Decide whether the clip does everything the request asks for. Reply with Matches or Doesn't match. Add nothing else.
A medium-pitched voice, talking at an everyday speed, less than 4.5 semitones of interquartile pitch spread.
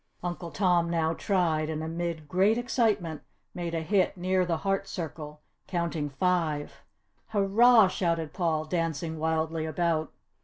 Doesn't match